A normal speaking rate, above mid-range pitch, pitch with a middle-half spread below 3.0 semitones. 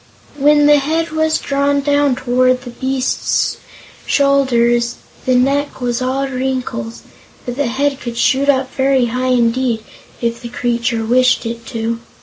Yes: average, 145 wpm; very high, 255 Hz; narrow, 2.6 semitones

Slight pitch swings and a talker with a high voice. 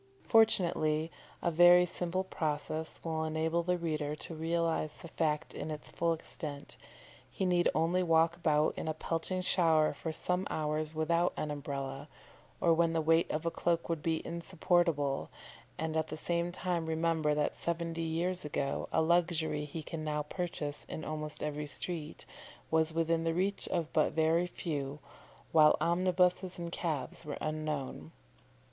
No: narrow, 1.9 semitones; medium, 160 Hz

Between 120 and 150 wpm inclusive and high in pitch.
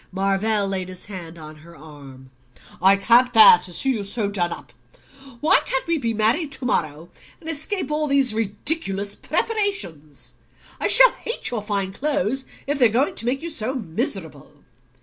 No: average, 170 wpm; high, 215 Hz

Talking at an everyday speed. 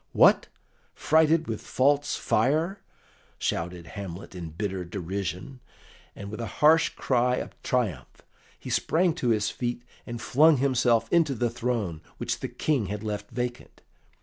Yes: average, 145 wpm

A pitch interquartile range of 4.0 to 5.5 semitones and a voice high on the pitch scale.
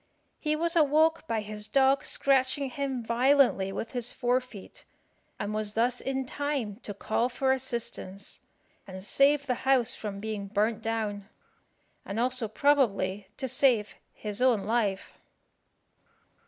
Yes: average, 4.3 semitones; high, 240 Hz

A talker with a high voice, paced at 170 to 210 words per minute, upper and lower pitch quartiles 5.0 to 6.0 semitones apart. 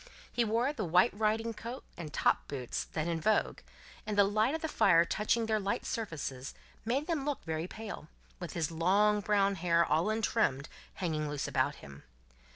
Yes: high, 200 Hz; average, 180 wpm; wide, 5.5 semitones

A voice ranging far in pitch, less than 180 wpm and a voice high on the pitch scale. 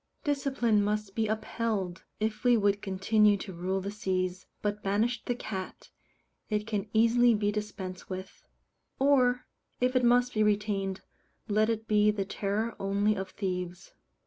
No: narrow, 2.5 semitones; average, 150 wpm; high, 210 Hz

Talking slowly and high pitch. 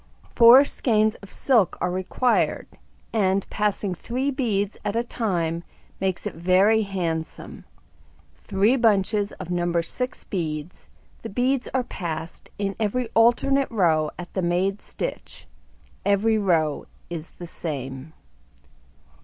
Yes: slow, 125 wpm; high, 195 Hz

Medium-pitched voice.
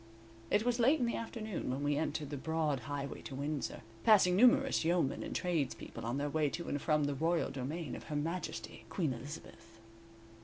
Yes: medium, 155 Hz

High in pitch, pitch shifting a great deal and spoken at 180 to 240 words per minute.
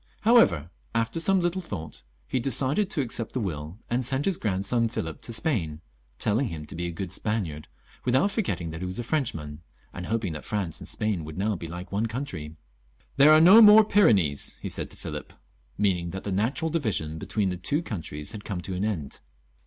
No: low, 105 Hz; wide, 8.0 semitones; fast, 205 wpm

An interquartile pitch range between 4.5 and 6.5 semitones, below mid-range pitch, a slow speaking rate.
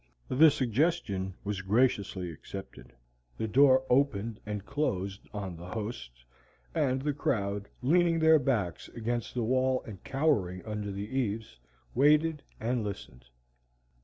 Yes: wide, 5.4 semitones; low, 110 Hz; slow, 130 wpm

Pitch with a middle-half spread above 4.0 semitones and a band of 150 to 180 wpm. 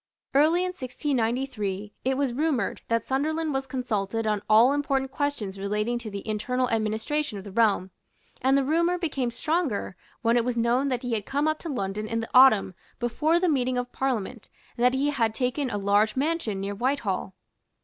No: average, 4.5 semitones; average, 190 wpm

